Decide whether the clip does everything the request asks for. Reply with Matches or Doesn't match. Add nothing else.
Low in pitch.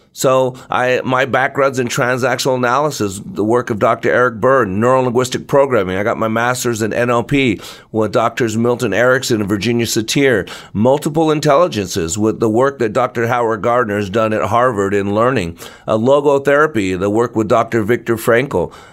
Matches